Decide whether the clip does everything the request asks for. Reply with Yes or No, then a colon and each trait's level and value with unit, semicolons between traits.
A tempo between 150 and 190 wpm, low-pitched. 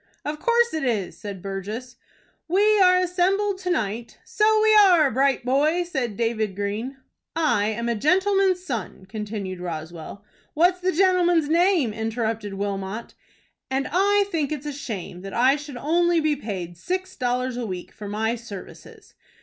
No: average, 160 wpm; very high, 260 Hz